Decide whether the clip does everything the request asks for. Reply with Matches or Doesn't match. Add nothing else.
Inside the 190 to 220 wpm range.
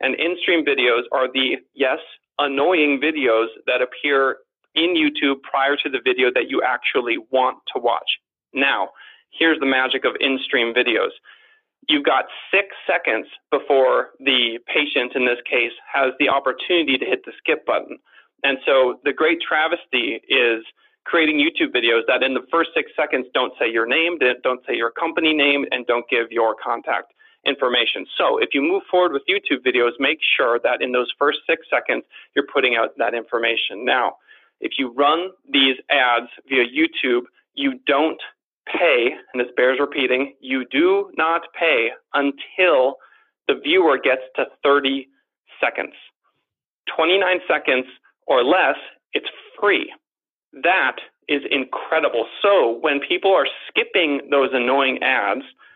Doesn't match